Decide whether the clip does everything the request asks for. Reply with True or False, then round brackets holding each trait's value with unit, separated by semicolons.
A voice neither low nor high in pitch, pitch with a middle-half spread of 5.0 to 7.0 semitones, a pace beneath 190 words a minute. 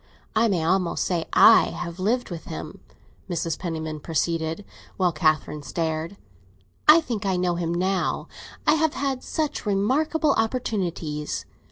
True (180 Hz; 5.4 semitones; 140 wpm)